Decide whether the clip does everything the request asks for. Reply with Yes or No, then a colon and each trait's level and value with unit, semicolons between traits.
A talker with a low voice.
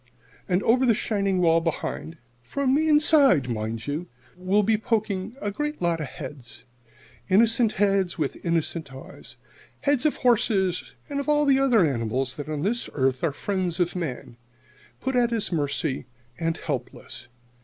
No: medium, 185 Hz